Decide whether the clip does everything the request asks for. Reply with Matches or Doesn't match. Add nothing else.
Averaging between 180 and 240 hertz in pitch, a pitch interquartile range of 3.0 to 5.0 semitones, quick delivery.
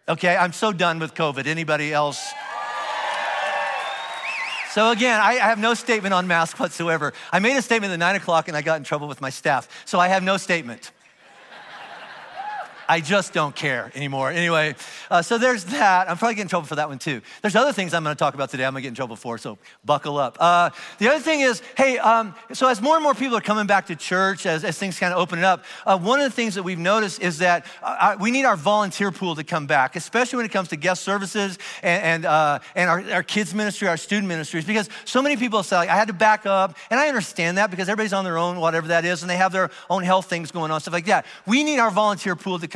Matches